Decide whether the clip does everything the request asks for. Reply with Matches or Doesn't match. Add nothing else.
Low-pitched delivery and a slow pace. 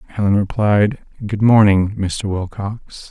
Matches